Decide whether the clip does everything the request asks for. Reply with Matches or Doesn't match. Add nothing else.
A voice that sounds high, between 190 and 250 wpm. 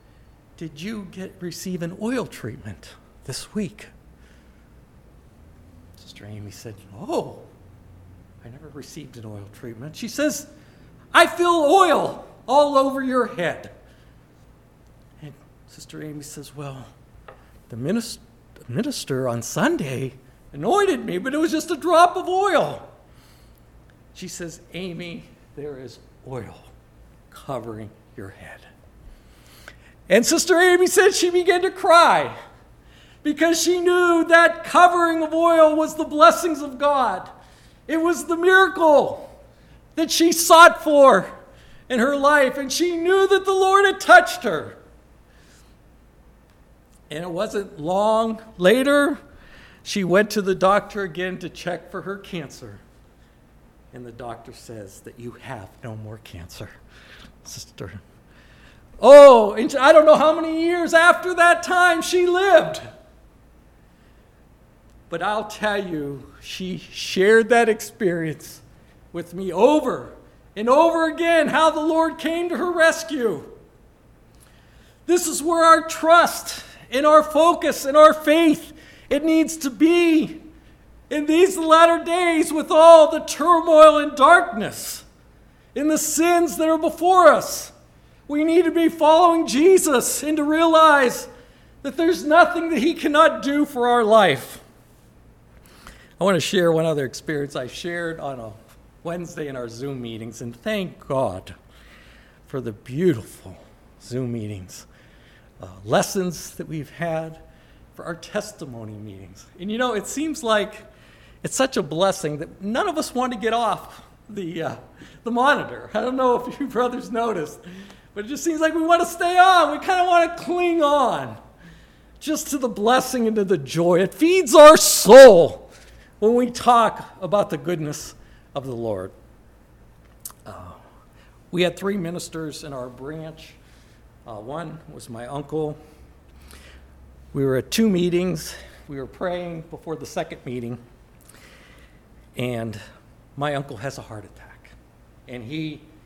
Doesn't match